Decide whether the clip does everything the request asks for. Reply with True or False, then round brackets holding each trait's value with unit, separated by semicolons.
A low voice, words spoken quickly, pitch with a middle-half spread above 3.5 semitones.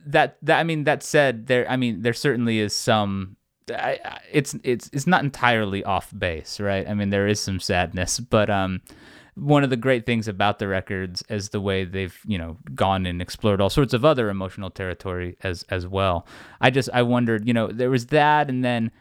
True (110 Hz; 210 wpm; 4.8 semitones)